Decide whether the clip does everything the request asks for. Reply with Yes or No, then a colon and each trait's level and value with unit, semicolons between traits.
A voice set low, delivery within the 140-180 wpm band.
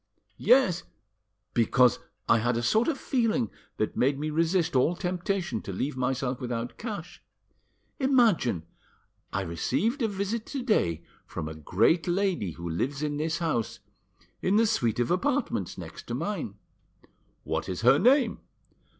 No: medium, 160 Hz; average, 145 wpm